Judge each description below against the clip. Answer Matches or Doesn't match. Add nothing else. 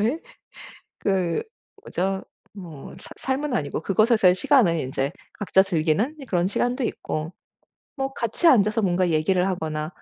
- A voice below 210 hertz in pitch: Matches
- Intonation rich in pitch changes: Matches